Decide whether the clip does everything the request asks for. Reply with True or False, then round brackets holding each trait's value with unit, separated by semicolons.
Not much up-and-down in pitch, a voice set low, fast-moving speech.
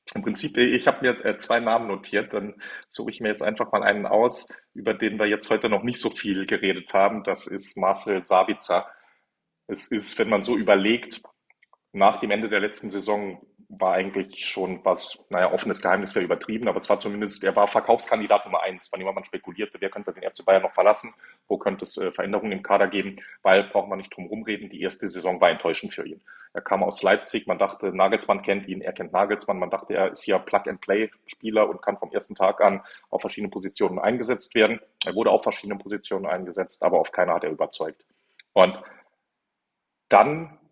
True (1.7 semitones; 105 Hz; 200 wpm)